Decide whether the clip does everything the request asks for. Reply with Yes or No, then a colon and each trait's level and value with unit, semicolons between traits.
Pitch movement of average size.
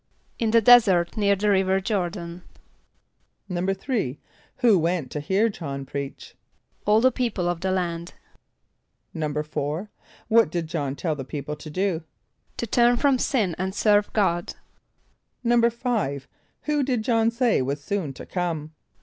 No: wide, 6.0 semitones